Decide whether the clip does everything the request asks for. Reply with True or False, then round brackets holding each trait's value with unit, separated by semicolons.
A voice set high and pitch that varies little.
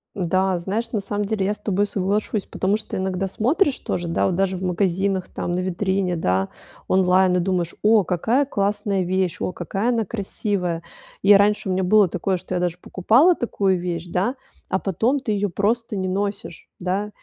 True (195 Hz; 2.3 semitones)